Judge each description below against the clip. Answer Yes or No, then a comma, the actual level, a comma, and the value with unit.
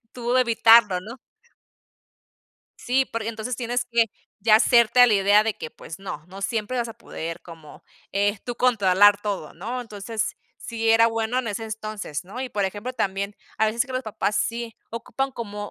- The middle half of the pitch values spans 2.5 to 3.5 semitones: Yes, average, 2.8 semitones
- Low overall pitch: No, high, 220 Hz